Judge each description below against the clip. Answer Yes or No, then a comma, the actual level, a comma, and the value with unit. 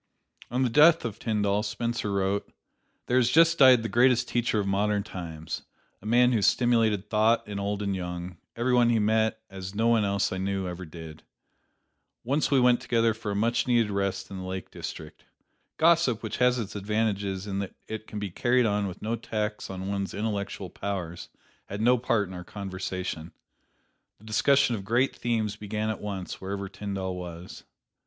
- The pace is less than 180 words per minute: No, average, 185 wpm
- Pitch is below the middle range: Yes, low, 105 Hz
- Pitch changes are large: No, average, 3.3 semitones